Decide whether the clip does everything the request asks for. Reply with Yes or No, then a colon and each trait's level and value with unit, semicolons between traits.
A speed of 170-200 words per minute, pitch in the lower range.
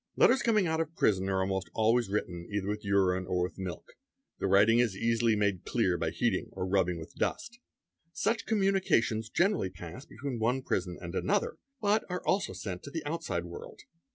Yes: average, 185 wpm; low, 110 Hz